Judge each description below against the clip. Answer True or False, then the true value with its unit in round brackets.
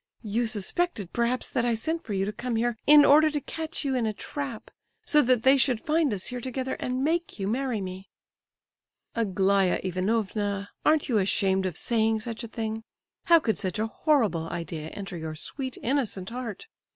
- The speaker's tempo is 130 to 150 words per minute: False (190 wpm)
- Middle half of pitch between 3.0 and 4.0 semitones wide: False (4.9 semitones)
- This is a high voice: True (230 Hz)